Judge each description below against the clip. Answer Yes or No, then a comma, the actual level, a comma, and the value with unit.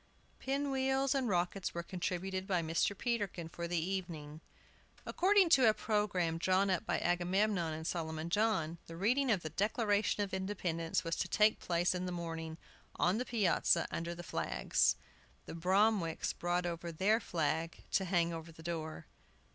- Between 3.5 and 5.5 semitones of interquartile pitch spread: Yes, average, 3.8 semitones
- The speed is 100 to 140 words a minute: No, average, 165 wpm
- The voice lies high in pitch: No, medium, 180 Hz